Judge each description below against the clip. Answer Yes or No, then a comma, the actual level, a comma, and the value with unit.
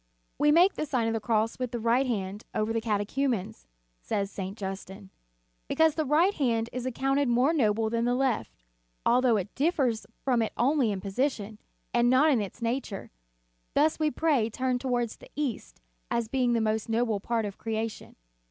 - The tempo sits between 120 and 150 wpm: No, average, 180 wpm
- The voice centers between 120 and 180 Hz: No, high, 235 Hz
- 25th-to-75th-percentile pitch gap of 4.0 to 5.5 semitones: No, average, 3.6 semitones